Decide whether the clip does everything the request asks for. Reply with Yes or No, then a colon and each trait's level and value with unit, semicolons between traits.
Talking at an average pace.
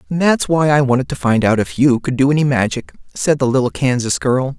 No: fast, 235 wpm